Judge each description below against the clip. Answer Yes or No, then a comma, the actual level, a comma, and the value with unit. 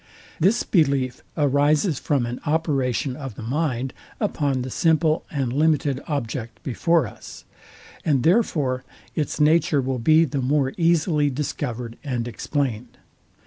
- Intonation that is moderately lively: Yes, average, 3.6 semitones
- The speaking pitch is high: No, medium, 140 Hz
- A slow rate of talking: Yes, slow, 130 wpm